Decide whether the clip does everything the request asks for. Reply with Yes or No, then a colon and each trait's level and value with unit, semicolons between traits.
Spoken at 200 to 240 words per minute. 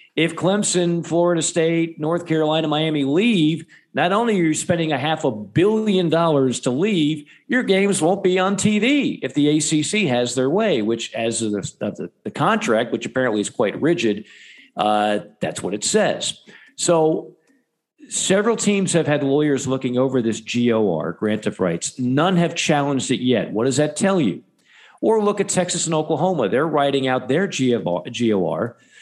No: average, 170 wpm